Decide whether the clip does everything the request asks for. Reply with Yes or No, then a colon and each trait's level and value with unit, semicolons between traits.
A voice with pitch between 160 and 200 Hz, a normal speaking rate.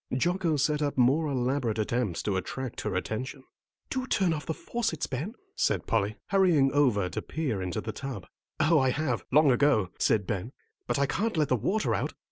No: low, 135 Hz; average, 190 wpm